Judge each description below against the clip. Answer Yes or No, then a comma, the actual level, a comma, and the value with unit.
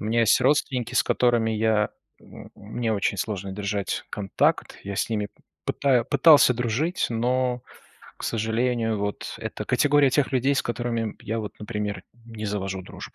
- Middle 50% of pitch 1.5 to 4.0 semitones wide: Yes, average, 3.1 semitones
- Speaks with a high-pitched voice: No, low, 115 Hz